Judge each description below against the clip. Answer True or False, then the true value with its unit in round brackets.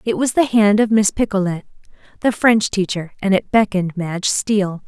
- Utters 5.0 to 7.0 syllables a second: True (5.4 syllables/s)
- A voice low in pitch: False (200 Hz)